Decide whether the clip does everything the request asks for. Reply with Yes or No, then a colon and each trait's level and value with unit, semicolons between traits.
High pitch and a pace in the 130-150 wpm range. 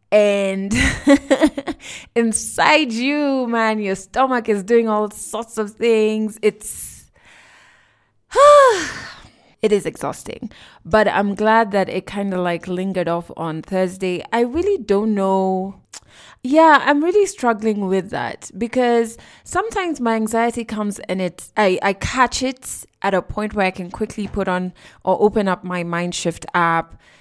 Yes: high, 215 Hz; average, 140 wpm